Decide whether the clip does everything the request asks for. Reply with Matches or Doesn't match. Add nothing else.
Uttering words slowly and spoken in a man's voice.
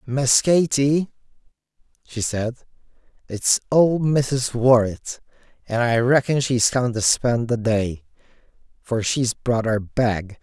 Matches